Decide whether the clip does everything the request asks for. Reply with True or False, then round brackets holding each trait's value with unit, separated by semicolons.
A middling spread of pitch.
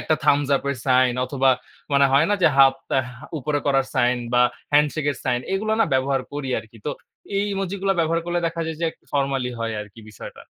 True (3.7 semitones)